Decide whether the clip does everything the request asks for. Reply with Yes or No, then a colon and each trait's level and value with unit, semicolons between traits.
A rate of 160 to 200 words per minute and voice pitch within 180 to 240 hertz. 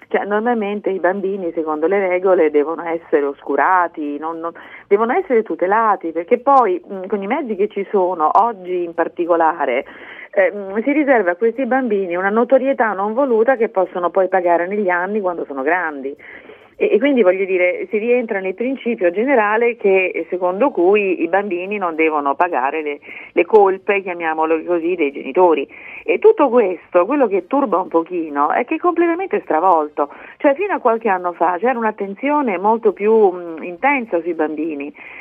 Yes: average, 165 wpm; high, 190 Hz